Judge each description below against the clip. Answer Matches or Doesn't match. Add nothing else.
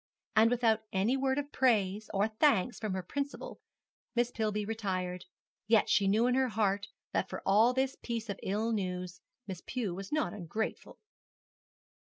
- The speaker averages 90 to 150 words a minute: Doesn't match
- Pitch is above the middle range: Matches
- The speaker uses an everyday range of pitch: Matches